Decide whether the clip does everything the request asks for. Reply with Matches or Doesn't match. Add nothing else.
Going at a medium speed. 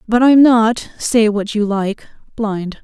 Matches